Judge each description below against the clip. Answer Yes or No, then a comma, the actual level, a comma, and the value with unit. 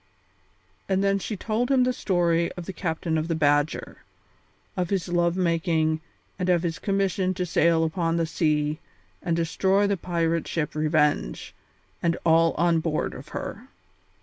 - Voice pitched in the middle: Yes, medium, 170 Hz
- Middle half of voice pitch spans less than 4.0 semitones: Yes, narrow, 2.5 semitones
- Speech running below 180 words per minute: Yes, average, 160 wpm